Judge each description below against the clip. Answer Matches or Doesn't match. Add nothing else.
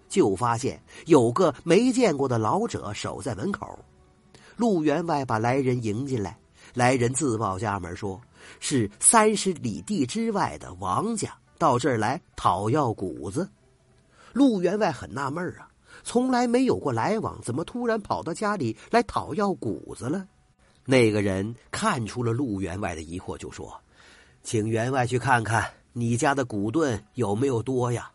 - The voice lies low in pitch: Matches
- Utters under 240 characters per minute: Matches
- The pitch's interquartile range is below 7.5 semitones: Doesn't match